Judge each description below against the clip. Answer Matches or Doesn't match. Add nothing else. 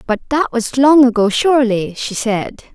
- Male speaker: Doesn't match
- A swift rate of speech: Doesn't match